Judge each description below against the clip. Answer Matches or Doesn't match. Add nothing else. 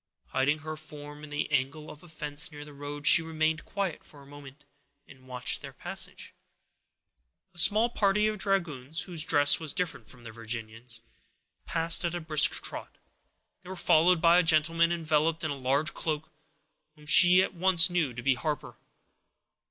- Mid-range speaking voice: Matches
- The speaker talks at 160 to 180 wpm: Matches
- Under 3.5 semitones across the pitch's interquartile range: Matches